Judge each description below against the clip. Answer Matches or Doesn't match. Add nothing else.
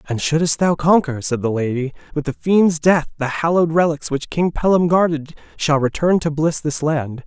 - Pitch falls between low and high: Matches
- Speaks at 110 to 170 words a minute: Doesn't match